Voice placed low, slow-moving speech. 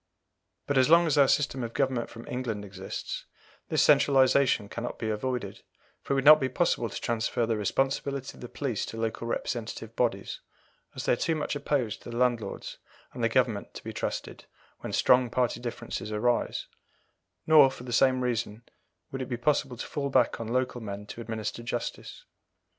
No: low, 120 Hz; average, 185 wpm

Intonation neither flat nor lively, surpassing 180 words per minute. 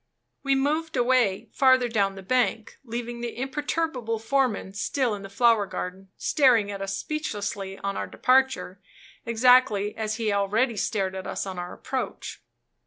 No: average, 4.6 semitones; average, 160 wpm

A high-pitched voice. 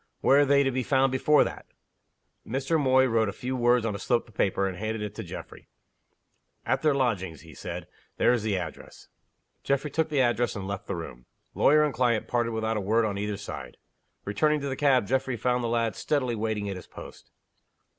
No: low, 120 Hz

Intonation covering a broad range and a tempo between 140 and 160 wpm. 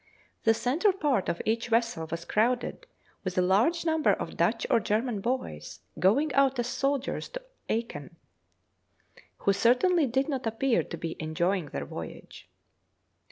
Yes: wide, 6.0 semitones; average, 150 wpm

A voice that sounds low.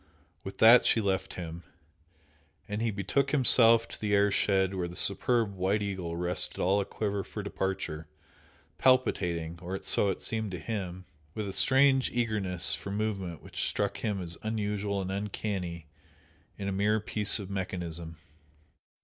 Yes: low, 100 Hz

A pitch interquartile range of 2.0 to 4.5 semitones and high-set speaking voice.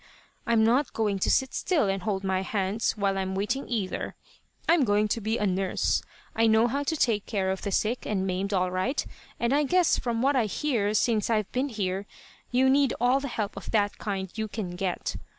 Yes: average, 4.1 semitones; high, 215 Hz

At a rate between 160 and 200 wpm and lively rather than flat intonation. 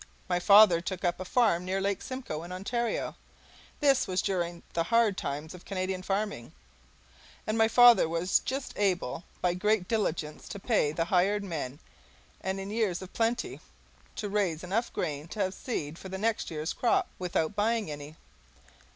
No: average, 170 wpm; average, 4.0 semitones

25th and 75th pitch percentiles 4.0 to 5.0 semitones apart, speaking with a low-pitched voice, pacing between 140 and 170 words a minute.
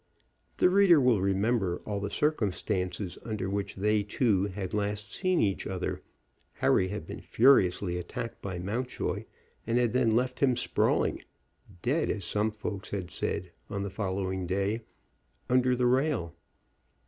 Yes: average, 4.5 semitones; low, 105 Hz; average, 150 wpm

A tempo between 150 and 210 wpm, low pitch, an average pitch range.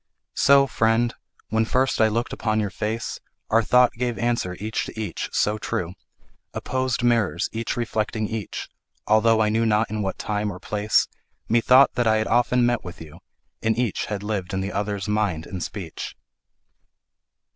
No: average, 170 wpm; low, 110 Hz; narrow, 2.3 semitones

